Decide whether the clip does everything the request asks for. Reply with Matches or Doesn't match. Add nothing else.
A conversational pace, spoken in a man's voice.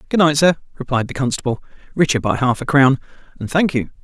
Matches